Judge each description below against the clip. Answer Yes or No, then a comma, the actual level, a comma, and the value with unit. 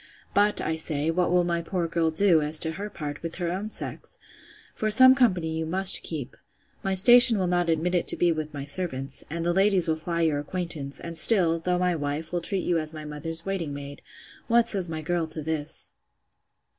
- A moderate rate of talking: No, fast, 210 wpm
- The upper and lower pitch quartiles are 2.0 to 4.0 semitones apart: Yes, average, 2.7 semitones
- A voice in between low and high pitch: Yes, medium, 170 Hz